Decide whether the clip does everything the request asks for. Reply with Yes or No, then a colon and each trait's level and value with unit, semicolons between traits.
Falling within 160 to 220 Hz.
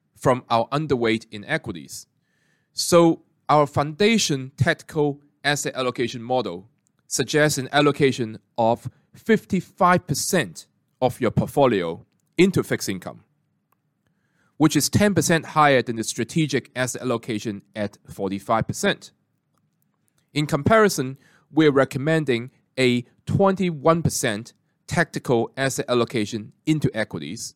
No: medium, 140 Hz